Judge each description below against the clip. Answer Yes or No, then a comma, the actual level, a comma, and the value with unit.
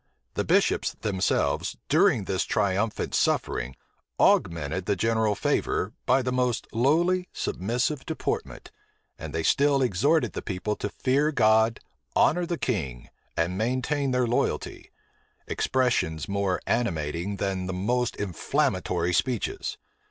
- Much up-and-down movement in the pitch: Yes, wide, 5.7 semitones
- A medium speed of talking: No, slow, 120 wpm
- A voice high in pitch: No, low, 110 Hz